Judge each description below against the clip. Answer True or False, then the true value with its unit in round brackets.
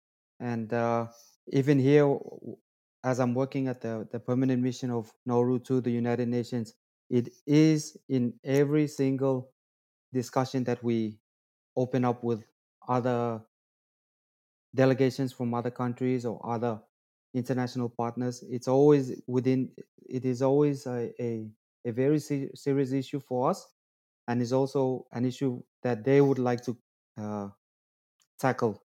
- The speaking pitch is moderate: False (125 Hz)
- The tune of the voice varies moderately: False (2.1 semitones)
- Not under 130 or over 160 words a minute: True (135 wpm)